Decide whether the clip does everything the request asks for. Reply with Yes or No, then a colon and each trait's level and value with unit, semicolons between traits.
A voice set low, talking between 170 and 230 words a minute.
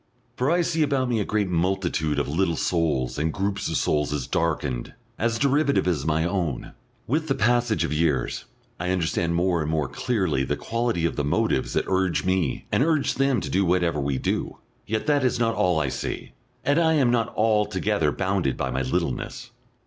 Yes: very low, 95 Hz; average, 195 wpm